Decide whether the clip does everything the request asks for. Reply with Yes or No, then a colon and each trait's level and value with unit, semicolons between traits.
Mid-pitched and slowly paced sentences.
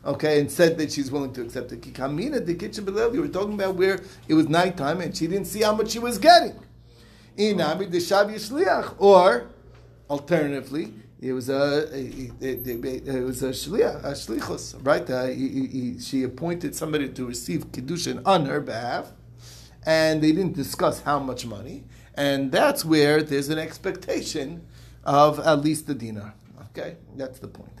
No: medium, 145 Hz; average, 160 wpm